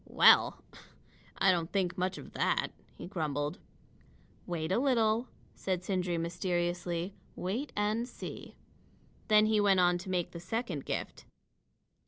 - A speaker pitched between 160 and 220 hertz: Yes, medium, 185 Hz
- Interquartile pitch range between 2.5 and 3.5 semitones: Yes, average, 3.2 semitones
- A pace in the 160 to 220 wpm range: No, slow, 135 wpm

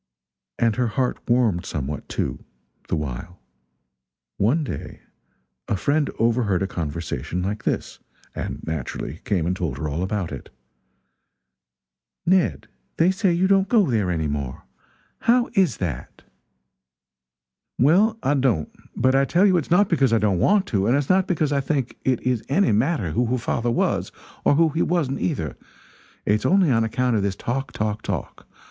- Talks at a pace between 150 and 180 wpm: Yes, average, 165 wpm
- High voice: No, low, 120 Hz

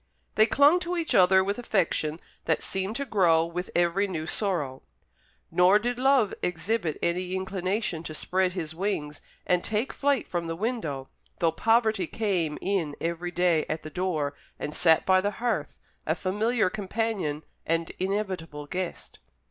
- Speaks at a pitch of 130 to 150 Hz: No, medium, 185 Hz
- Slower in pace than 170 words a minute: Yes, average, 155 wpm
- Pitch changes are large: No, average, 4.5 semitones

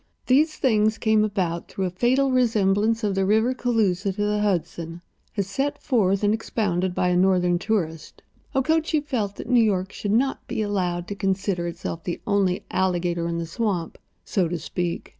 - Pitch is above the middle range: Yes, high, 200 Hz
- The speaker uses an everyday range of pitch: Yes, average, 3.9 semitones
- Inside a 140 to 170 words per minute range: No, average, 180 wpm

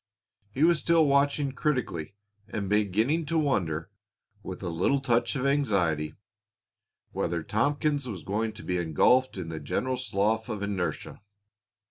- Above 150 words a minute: No, average, 140 wpm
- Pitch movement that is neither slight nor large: No, wide, 7.2 semitones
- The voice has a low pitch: Yes, low, 110 Hz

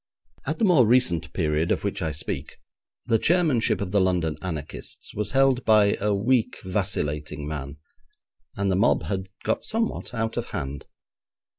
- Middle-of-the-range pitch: No, low, 100 Hz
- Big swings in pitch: Yes, wide, 6.4 semitones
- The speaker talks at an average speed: Yes, average, 160 wpm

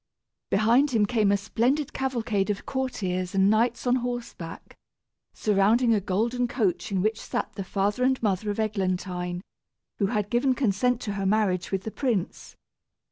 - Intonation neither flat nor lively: Yes, average, 3.9 semitones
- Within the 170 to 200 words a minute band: No, average, 160 wpm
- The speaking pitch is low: No, high, 215 Hz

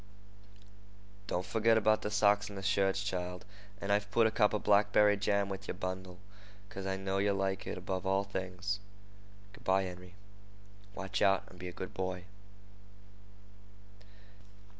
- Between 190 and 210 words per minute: No, average, 160 wpm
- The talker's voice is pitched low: Yes, very low, 95 Hz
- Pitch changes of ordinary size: No, narrow, 1.5 semitones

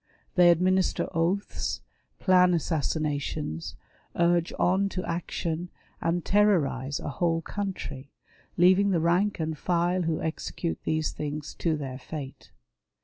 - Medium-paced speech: No, slow, 120 wpm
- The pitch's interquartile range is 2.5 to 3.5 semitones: Yes, average, 2.9 semitones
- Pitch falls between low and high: Yes, medium, 170 Hz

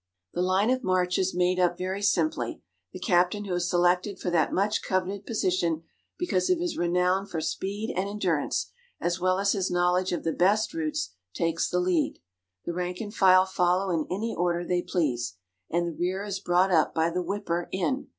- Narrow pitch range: Yes, narrow, 2.1 semitones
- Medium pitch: Yes, medium, 180 Hz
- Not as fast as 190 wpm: No, average, 195 wpm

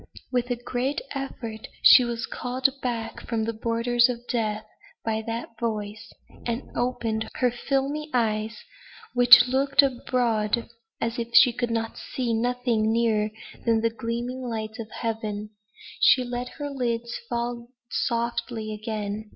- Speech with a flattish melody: Yes, narrow, 1.9 semitones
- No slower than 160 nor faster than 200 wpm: No, slow, 135 wpm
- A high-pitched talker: Yes, high, 235 Hz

